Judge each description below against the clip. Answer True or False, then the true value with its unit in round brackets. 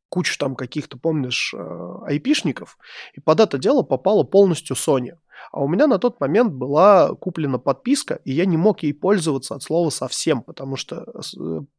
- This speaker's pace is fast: True (165 wpm)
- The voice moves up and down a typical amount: False (6.5 semitones)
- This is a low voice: False (155 Hz)